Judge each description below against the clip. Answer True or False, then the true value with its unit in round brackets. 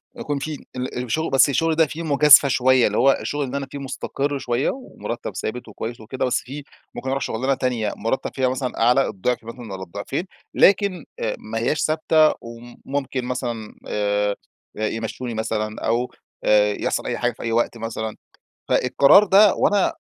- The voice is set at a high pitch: False (125 Hz)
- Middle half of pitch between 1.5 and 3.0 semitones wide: False (3.8 semitones)